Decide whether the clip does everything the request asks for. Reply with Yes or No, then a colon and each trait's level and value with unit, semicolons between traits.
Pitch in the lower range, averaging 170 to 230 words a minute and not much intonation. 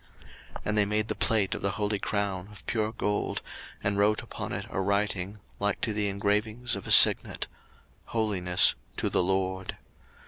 Yes: low, 100 Hz; average, 175 wpm; narrow, 1.6 semitones